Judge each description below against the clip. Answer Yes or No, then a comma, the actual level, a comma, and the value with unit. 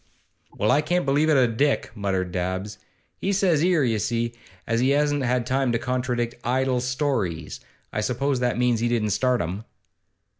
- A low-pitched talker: Yes, low, 125 Hz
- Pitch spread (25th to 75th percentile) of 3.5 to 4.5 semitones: Yes, average, 3.9 semitones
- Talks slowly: No, average, 175 wpm